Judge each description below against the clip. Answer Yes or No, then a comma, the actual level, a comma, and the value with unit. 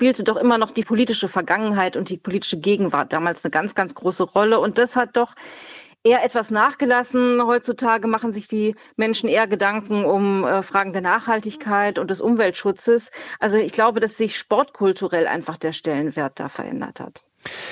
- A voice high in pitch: Yes, high, 215 Hz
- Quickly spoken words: No, average, 170 wpm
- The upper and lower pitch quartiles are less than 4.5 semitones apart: Yes, average, 3.3 semitones